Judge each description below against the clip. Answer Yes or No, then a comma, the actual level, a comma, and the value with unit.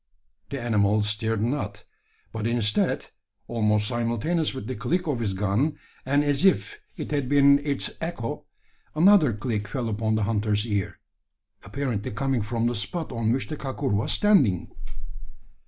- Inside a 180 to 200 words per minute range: No, average, 155 wpm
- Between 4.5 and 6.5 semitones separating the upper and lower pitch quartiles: Yes, average, 4.9 semitones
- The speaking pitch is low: Yes, low, 120 Hz